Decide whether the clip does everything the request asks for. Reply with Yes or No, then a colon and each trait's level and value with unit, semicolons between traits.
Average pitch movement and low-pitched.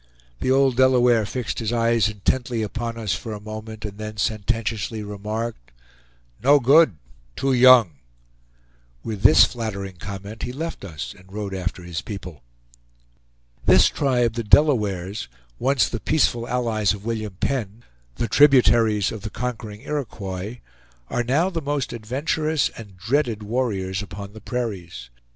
Yes: average, 3.7 semitones; low, 110 Hz